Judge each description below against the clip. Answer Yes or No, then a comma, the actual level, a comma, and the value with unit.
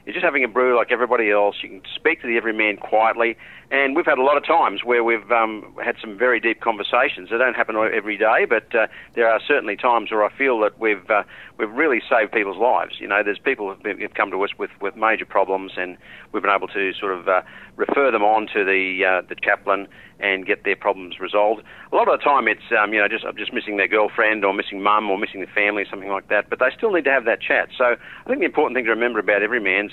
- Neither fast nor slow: No, fast, 260 wpm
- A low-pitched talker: Yes, low, 105 Hz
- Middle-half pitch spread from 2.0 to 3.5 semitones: Yes, average, 2.9 semitones